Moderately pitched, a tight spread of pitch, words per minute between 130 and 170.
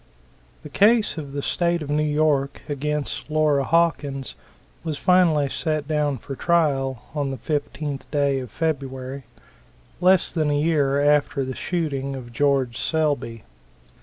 Yes: medium, 145 Hz; narrow, 2.3 semitones; average, 140 wpm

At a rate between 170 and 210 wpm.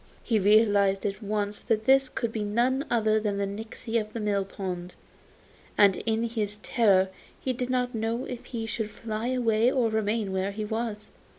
Yes: average, 180 wpm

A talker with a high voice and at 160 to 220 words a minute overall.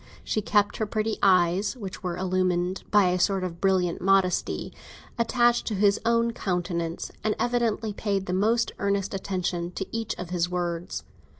Yes: high, 195 Hz; average, 165 wpm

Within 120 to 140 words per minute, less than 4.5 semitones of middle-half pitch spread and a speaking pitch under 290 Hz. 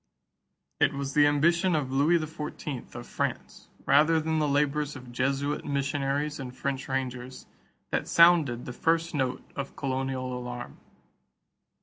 Yes: slow, 135 wpm; narrow, 2.6 semitones; medium, 140 Hz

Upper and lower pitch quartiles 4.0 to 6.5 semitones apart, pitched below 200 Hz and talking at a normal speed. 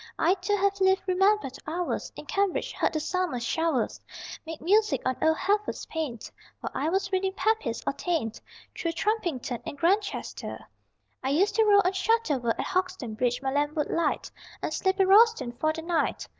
No: wide, 5.4 semitones; very high, 350 Hz; average, 180 wpm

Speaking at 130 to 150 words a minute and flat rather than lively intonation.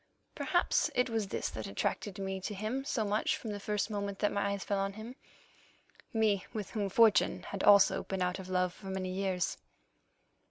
No: average, 190 wpm; narrow, 2.0 semitones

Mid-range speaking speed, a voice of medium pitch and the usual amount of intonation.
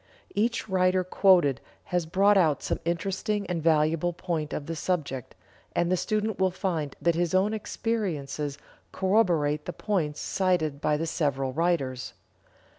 Yes: average, 145 wpm; medium, 175 Hz; average, 3.9 semitones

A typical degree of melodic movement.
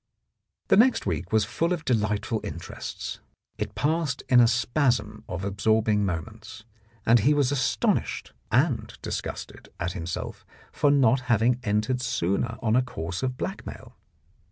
Yes: average, 4.0 semitones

